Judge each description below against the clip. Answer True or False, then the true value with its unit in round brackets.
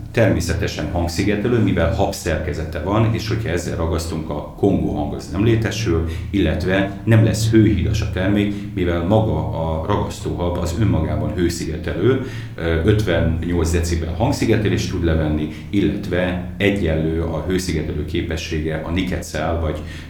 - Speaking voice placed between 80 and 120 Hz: True (90 Hz)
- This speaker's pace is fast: False (125 wpm)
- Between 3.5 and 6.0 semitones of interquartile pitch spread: True (4.0 semitones)